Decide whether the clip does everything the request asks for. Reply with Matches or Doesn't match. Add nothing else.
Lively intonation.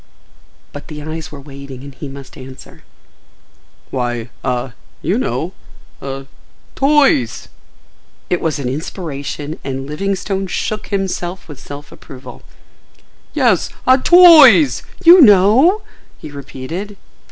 Matches